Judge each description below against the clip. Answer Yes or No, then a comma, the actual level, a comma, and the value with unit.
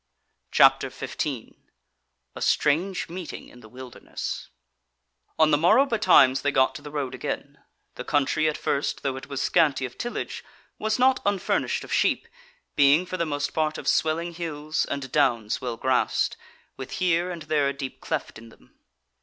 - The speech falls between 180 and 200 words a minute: No, average, 170 wpm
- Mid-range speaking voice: Yes, medium, 150 Hz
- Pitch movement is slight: No, average, 4.2 semitones